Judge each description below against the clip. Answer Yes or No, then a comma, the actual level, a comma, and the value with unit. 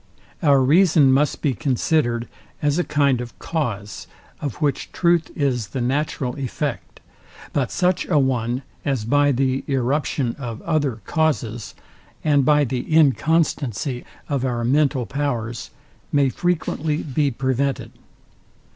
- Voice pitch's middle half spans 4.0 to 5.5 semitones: No, average, 3.4 semitones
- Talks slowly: Yes, slow, 130 wpm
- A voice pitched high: No, medium, 140 Hz